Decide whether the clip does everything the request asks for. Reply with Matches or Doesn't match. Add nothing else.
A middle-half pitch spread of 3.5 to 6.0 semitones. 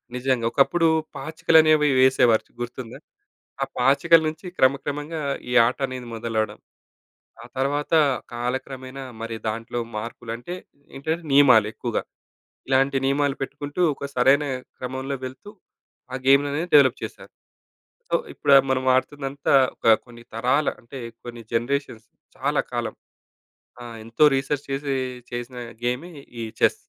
Doesn't match